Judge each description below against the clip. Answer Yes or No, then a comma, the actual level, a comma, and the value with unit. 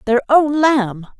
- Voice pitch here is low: No, very high, 255 Hz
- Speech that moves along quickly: No, average, 150 wpm